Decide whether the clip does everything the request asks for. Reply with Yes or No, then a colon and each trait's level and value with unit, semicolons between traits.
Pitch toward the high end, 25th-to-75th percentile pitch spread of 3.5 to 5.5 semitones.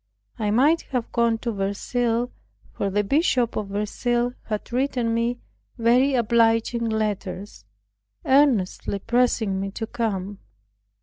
No: high, 230 Hz; average, 3.0 semitones